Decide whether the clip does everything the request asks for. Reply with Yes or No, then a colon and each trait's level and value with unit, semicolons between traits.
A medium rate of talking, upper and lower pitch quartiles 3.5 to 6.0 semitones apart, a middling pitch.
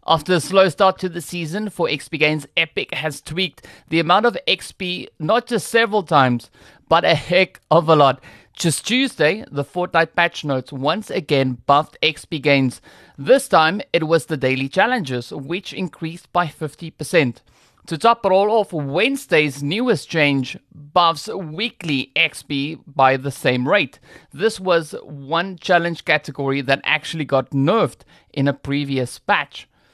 Yes: average, 155 wpm; average, 4.6 semitones; medium, 160 Hz